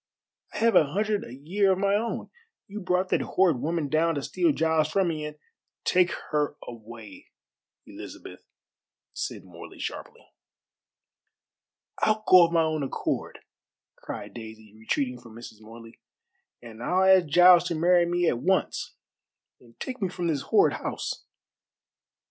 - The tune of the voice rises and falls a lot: Yes, wide, 6.7 semitones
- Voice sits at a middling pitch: Yes, medium, 165 Hz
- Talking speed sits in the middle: Yes, average, 155 wpm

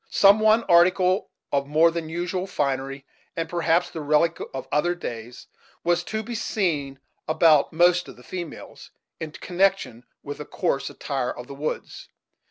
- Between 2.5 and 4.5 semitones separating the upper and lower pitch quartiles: Yes, average, 4.1 semitones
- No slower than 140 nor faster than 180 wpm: Yes, average, 160 wpm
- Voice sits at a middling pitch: Yes, medium, 165 Hz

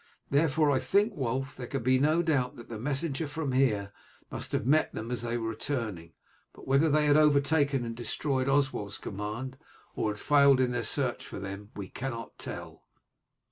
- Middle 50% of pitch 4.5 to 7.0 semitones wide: No, average, 3.8 semitones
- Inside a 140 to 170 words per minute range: No, average, 185 wpm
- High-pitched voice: No, low, 130 Hz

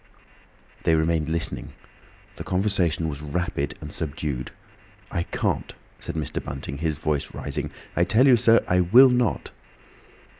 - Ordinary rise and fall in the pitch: Yes, average, 3.9 semitones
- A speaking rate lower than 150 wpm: Yes, average, 140 wpm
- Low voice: Yes, very low, 80 Hz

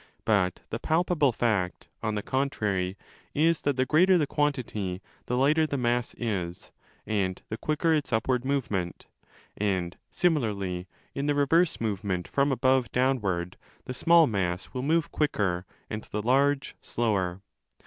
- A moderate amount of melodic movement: No, wide, 6.5 semitones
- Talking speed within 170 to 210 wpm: No, average, 150 wpm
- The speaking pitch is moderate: No, low, 120 Hz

